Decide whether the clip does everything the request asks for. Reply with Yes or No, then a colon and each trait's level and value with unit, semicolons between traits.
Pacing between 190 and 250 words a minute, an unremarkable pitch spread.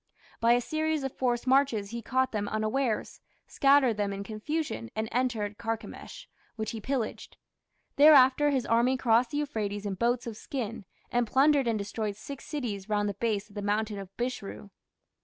No: average, 175 wpm; average, 4.0 semitones